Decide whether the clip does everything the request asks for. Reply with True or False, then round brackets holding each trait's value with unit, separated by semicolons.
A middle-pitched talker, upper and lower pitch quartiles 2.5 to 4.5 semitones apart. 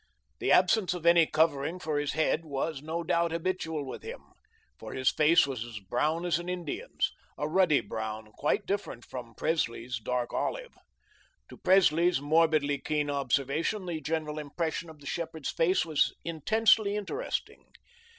True (160 Hz; 3.4 semitones)